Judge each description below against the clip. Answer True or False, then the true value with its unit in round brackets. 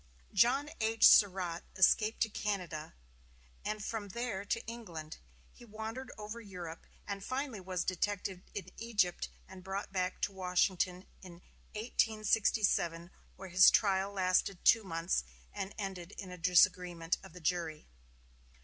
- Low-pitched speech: False (190 Hz)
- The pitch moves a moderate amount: True (3.0 semitones)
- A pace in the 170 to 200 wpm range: False (135 wpm)